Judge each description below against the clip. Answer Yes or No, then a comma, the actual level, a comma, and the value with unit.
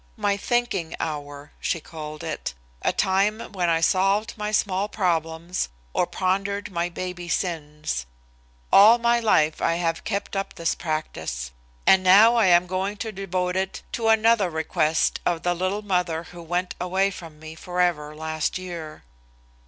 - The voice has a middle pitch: Yes, medium, 180 Hz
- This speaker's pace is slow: No, average, 155 wpm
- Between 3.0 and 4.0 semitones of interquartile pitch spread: Yes, average, 3.5 semitones